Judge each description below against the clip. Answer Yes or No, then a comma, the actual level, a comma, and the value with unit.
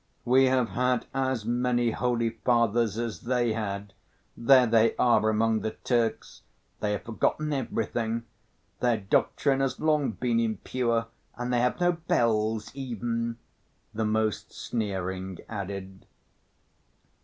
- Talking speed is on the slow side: Yes, slow, 125 wpm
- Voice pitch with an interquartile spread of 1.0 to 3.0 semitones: Yes, narrow, 2.4 semitones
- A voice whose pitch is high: No, low, 115 Hz